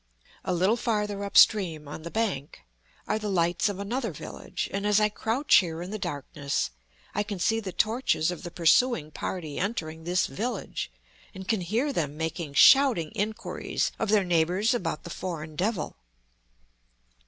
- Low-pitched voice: No, high, 190 Hz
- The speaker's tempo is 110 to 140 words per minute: No, average, 165 wpm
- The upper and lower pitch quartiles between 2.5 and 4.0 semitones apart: No, average, 4.9 semitones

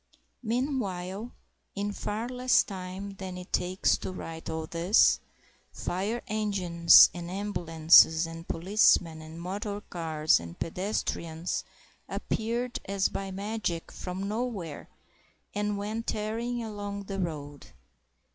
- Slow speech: Yes, slow, 115 wpm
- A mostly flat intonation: No, average, 3.9 semitones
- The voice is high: Yes, high, 195 Hz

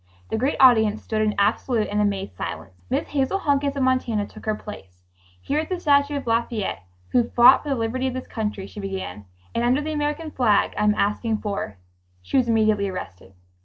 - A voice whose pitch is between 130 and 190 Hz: No, high, 225 Hz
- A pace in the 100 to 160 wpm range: No, fast, 205 wpm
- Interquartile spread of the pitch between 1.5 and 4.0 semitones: No, average, 4.7 semitones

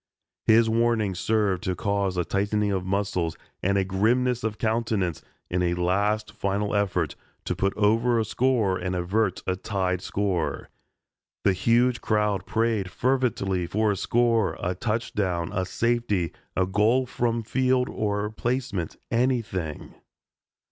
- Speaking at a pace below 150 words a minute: Yes, average, 140 wpm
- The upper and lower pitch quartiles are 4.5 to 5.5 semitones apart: No, average, 3.7 semitones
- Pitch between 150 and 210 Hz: No, low, 105 Hz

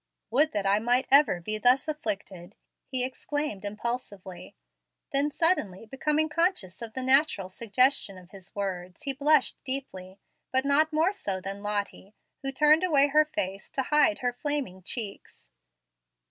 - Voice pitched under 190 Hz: No, very high, 255 Hz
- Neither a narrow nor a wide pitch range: No, wide, 7.0 semitones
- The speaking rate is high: No, average, 150 wpm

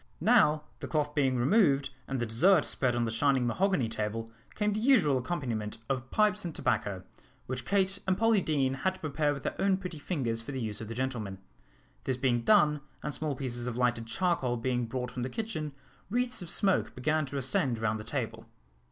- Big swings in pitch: Yes, wide, 6.6 semitones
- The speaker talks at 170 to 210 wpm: Yes, fast, 205 wpm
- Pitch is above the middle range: No, low, 135 Hz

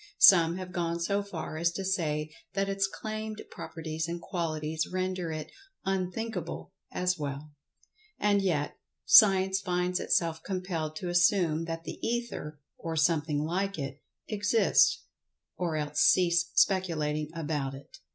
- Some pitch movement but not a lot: Yes, average, 3.4 semitones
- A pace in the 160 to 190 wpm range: No, slow, 135 wpm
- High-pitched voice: No, medium, 170 Hz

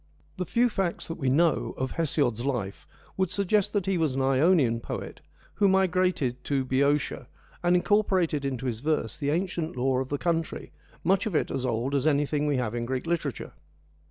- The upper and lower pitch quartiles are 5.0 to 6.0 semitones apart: Yes, average, 5.3 semitones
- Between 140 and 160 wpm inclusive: No, average, 185 wpm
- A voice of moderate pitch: Yes, medium, 150 Hz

